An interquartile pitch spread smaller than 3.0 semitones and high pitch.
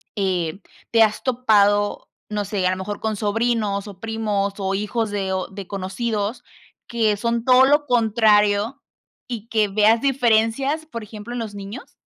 Yes: narrow, 2.6 semitones; high, 215 Hz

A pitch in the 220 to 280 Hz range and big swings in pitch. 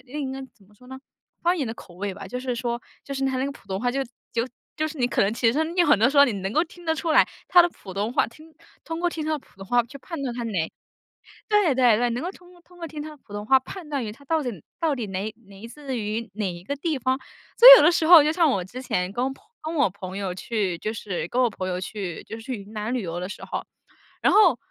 Yes: very high, 250 Hz; wide, 6.7 semitones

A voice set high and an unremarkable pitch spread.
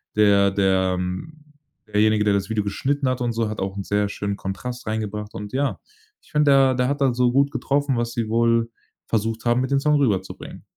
No: low, 115 Hz; average, 4.1 semitones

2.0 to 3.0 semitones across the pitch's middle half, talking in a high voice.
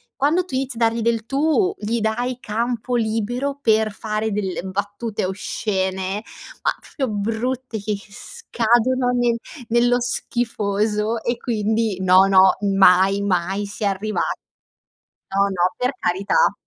No: average, 3.4 semitones; high, 220 Hz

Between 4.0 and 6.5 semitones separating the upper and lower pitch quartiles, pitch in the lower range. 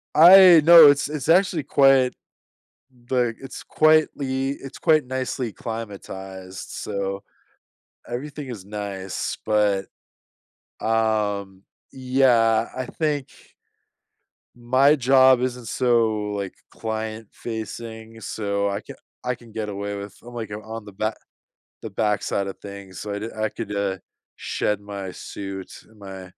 Yes: average, 4.4 semitones; low, 110 Hz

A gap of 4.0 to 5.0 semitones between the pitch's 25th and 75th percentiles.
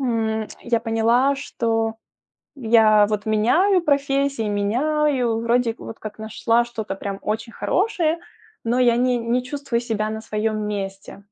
No: average, 2.7 semitones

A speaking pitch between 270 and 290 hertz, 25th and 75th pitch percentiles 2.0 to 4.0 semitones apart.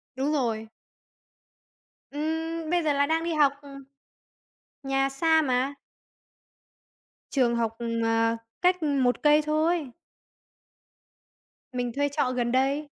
Yes: very high, 280 Hz; average, 3.7 semitones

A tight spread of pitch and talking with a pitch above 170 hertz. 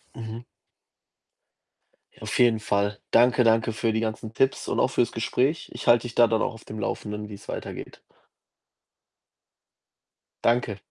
No: narrow, 1.8 semitones; low, 115 Hz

